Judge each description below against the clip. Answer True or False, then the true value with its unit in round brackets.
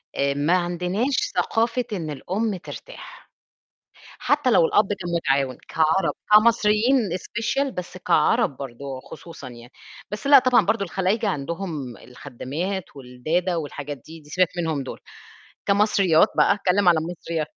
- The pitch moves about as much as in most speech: False (6.1 semitones)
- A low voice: False (175 Hz)